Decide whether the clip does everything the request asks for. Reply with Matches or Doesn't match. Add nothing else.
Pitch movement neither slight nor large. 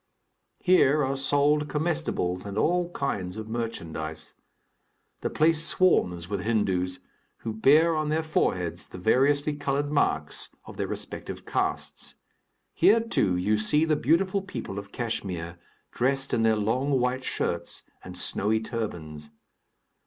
Doesn't match